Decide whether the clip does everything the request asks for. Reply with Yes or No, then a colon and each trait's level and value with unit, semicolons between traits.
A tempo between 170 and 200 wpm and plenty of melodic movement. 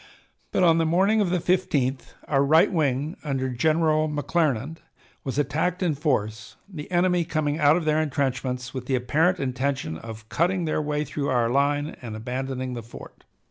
No: average, 175 wpm; average, 3.9 semitones